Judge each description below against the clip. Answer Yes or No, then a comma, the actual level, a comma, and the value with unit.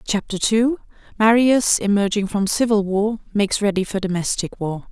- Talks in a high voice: Yes, high, 210 Hz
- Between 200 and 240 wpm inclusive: No, slow, 135 wpm